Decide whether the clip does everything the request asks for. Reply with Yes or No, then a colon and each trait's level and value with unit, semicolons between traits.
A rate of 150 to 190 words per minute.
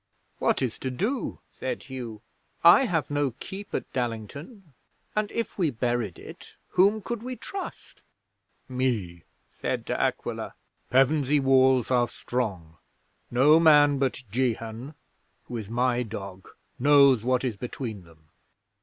No: slow, 135 wpm